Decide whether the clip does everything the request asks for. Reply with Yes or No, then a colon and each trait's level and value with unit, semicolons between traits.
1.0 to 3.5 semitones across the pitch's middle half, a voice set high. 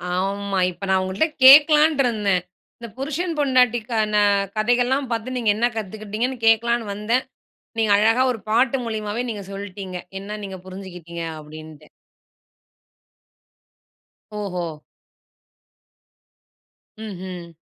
No: average, 4.2 semitones; high, 215 Hz